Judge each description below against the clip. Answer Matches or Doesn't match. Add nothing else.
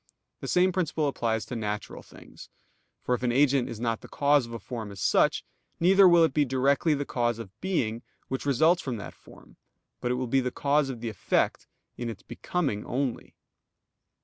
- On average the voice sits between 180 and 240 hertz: Doesn't match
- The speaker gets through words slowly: Doesn't match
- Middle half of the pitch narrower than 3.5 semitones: Doesn't match